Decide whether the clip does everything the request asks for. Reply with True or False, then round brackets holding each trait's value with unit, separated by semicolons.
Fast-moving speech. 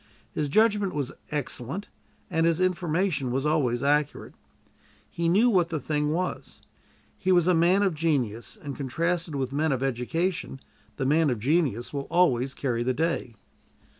False (160 wpm)